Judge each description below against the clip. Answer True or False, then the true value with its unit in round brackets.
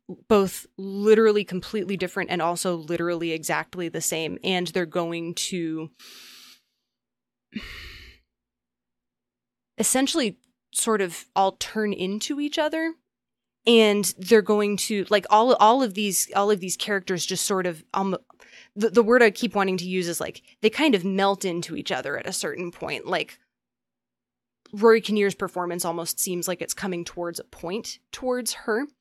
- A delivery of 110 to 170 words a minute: True (155 wpm)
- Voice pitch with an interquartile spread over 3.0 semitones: True (3.6 semitones)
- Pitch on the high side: True (195 Hz)